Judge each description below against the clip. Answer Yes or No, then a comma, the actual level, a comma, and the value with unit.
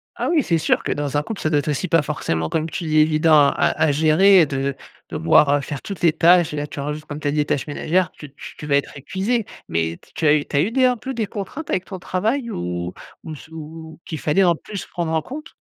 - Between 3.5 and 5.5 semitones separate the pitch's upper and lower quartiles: Yes, average, 4.2 semitones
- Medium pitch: Yes, medium, 155 Hz